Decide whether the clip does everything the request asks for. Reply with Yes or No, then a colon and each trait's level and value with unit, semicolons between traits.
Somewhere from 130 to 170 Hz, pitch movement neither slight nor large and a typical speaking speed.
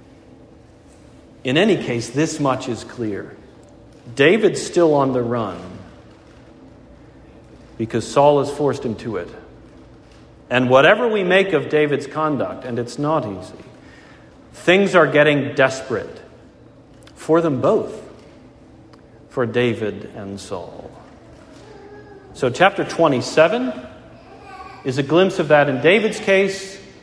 No: low, 135 Hz; average, 4.9 semitones; slow, 115 wpm